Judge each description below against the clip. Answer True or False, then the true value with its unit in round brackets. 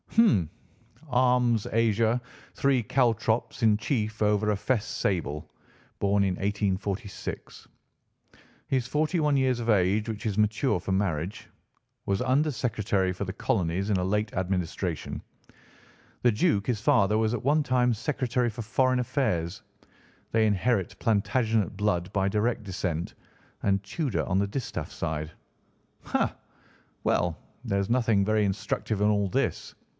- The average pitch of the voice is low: True (105 Hz)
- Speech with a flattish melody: False (3.8 semitones)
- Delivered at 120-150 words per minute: True (140 wpm)